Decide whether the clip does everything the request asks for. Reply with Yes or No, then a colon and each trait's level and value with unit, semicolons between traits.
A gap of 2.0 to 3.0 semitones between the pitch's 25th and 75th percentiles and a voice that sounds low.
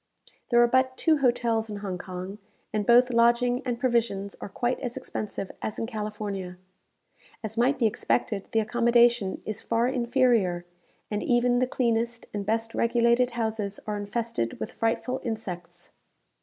No: average, 2.7 semitones; high, 230 Hz